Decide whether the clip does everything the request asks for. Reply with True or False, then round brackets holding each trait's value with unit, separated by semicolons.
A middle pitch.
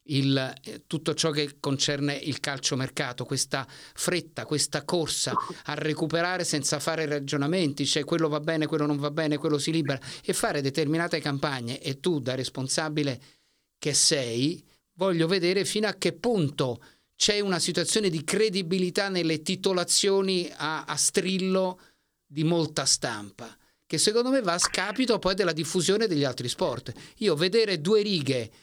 True (160 Hz)